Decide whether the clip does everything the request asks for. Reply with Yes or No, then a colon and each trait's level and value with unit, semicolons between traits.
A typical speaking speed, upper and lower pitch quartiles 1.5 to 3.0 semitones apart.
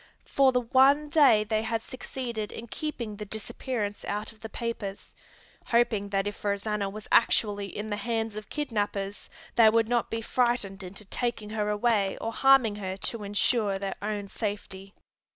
Yes: average, 170 wpm; narrow, 2.5 semitones